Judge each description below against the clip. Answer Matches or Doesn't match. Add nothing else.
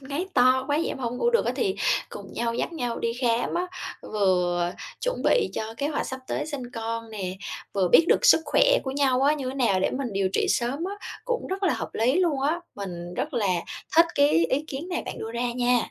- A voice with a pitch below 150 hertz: Doesn't match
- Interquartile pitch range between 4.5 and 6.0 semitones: Matches